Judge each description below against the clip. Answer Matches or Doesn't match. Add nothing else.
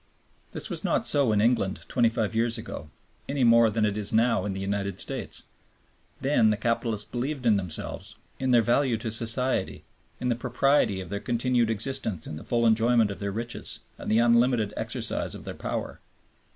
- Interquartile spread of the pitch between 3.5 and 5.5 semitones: Doesn't match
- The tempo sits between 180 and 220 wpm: Matches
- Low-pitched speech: Matches